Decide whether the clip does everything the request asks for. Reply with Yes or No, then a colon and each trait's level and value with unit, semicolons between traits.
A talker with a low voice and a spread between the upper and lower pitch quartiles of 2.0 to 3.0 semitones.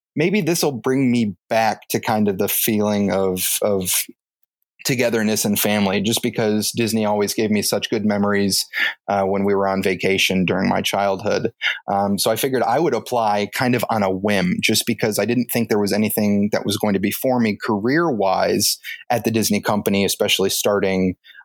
Yes: low, 105 Hz; narrow, 2.6 semitones